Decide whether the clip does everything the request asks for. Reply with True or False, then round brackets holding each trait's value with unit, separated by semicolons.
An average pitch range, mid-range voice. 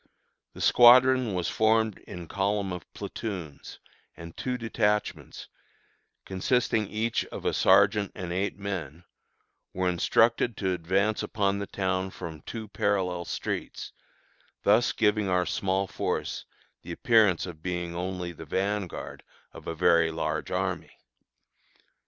False (3.2 semitones; 95 Hz)